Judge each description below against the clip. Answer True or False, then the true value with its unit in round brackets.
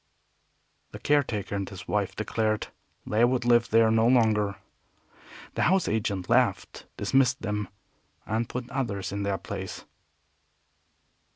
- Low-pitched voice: True (110 Hz)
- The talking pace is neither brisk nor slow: False (125 wpm)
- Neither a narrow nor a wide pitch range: True (3.1 semitones)